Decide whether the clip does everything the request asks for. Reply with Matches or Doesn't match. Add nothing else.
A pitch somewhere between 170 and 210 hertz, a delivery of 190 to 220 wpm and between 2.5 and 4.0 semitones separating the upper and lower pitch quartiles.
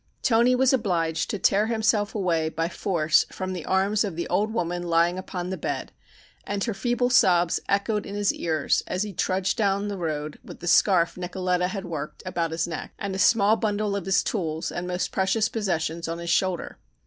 Matches